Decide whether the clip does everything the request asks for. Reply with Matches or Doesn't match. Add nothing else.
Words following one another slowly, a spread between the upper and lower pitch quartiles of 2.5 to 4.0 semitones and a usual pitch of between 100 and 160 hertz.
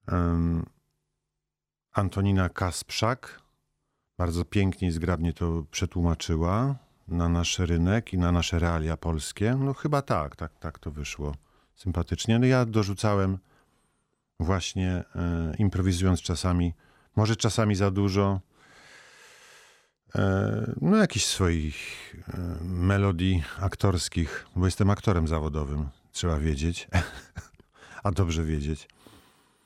Doesn't match